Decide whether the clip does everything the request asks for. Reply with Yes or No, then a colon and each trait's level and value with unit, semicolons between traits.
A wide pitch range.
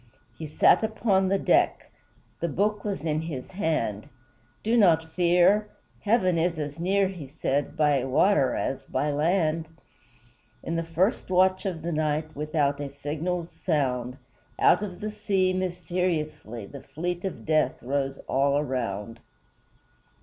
No: average, 4.5 semitones